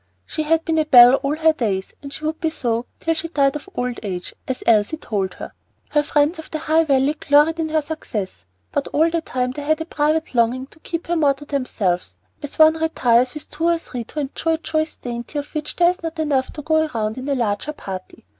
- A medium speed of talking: No, fast, 240 wpm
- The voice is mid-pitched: No, very high, 295 Hz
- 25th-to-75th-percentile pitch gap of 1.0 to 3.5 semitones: No, average, 4.2 semitones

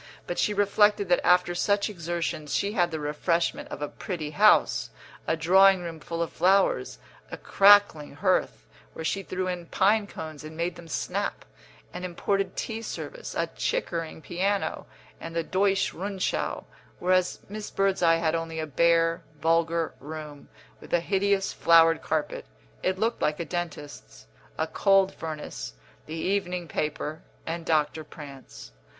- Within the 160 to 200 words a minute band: No, average, 150 wpm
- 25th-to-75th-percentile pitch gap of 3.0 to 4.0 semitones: Yes, average, 3.3 semitones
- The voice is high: No, medium, 170 Hz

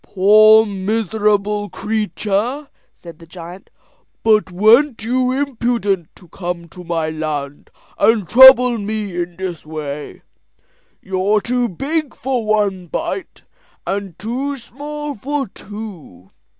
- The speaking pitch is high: Yes, high, 210 Hz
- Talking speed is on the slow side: Yes, slow, 115 wpm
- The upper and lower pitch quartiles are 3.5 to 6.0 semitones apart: Yes, average, 5.3 semitones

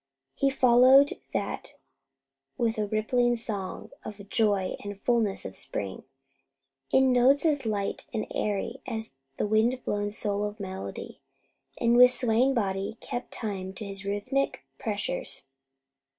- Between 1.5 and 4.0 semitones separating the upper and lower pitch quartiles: Yes, average, 3.5 semitones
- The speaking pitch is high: Yes, high, 220 Hz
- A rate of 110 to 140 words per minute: Yes, slow, 135 wpm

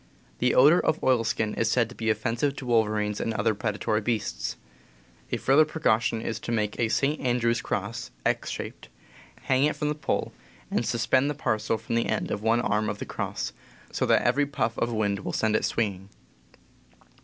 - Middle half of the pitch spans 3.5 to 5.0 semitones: No, average, 2.9 semitones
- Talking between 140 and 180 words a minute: No, average, 190 wpm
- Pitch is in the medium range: No, low, 115 Hz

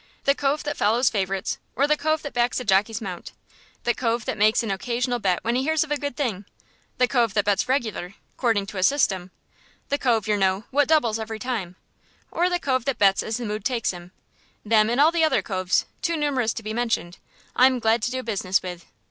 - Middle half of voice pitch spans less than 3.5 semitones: No, average, 4.7 semitones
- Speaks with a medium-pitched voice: No, high, 230 Hz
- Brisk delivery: Yes, fast, 225 wpm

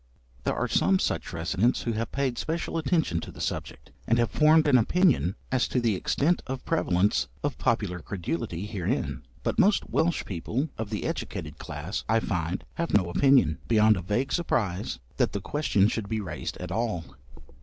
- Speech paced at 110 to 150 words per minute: No, average, 180 wpm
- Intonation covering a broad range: Yes, wide, 6.8 semitones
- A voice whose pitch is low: Yes, low, 110 Hz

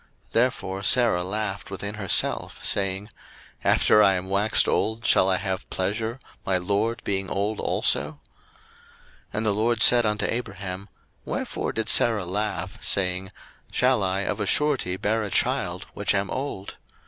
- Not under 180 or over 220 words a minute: No, average, 155 wpm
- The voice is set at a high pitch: No, low, 100 Hz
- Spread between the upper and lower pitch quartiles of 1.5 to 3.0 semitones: Yes, narrow, 2.6 semitones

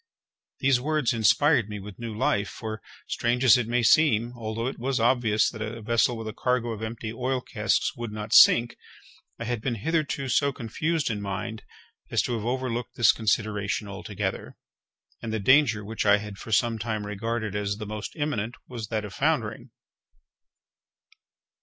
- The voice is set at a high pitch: No, low, 115 Hz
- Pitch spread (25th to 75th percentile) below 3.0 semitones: Yes, narrow, 2.6 semitones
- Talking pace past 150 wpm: Yes, average, 175 wpm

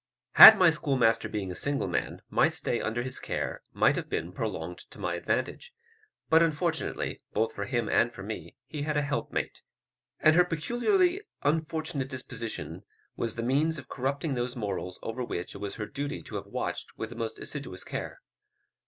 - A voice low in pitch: Yes, low, 130 Hz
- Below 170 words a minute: No, average, 180 wpm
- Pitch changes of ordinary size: No, wide, 6.0 semitones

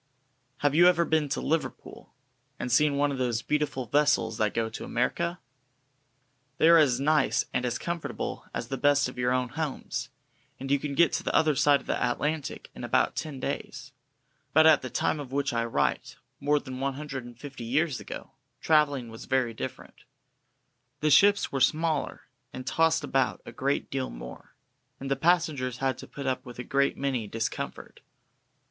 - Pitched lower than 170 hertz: Yes, medium, 140 Hz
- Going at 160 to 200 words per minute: Yes, average, 190 wpm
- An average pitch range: Yes, average, 3.2 semitones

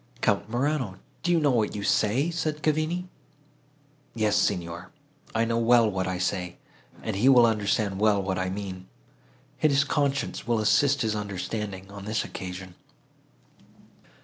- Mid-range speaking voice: No, low, 105 Hz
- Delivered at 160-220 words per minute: No, average, 150 wpm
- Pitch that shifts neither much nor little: No, wide, 6.0 semitones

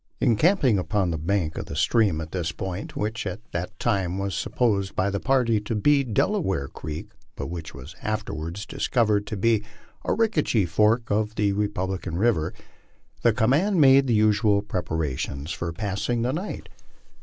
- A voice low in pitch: Yes, low, 105 Hz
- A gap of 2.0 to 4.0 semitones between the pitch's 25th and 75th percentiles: No, average, 4.7 semitones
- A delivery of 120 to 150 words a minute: No, average, 160 wpm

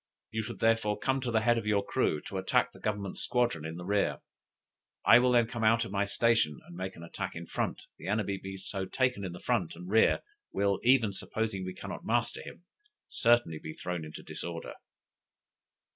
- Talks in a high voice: No, low, 100 Hz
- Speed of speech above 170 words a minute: Yes, fast, 205 wpm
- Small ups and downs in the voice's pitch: No, average, 3.9 semitones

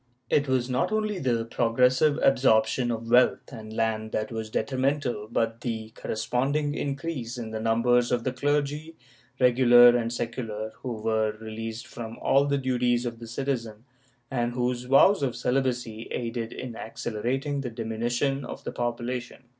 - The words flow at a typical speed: Yes, average, 155 wpm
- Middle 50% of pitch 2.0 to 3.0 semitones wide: Yes, narrow, 2.6 semitones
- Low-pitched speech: Yes, low, 120 Hz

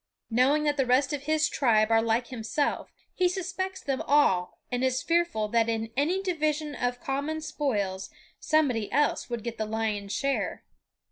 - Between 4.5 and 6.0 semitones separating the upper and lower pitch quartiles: Yes, average, 5.2 semitones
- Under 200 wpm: Yes, average, 165 wpm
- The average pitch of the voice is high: Yes, very high, 265 Hz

